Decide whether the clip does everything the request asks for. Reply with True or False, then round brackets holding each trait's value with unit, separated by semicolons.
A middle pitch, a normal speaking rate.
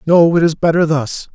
False (160 Hz; 220 wpm)